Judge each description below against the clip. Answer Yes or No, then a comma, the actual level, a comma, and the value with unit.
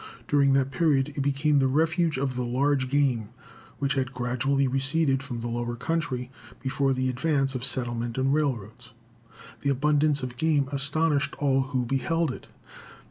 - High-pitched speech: No, low, 135 Hz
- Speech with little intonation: Yes, narrow, 2.1 semitones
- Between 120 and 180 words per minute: Yes, average, 160 wpm